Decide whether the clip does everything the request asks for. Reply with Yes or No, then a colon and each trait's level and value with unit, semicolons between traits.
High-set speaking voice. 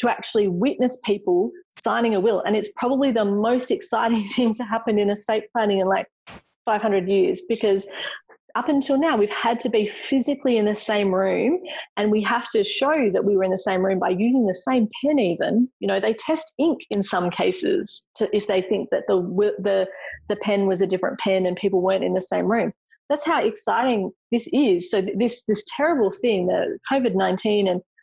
Yes: high, 220 Hz